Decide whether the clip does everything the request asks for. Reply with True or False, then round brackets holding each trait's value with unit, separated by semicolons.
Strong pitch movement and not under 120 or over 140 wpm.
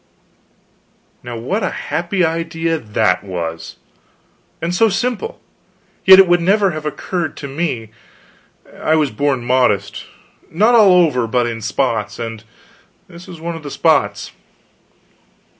True (7.1 semitones; 135 wpm)